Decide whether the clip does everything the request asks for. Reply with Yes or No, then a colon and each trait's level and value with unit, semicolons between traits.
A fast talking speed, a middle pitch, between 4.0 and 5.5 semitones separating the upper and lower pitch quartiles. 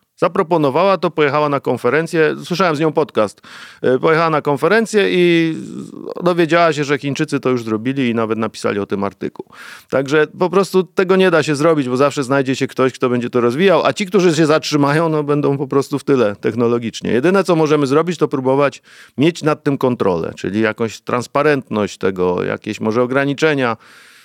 Yes: fast, 180 wpm; medium, 145 Hz; average, 4.5 semitones